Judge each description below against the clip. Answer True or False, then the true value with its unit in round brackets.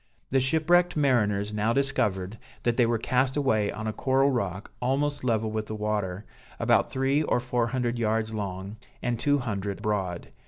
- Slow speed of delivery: False (170 wpm)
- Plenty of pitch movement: False (4.1 semitones)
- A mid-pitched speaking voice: False (115 Hz)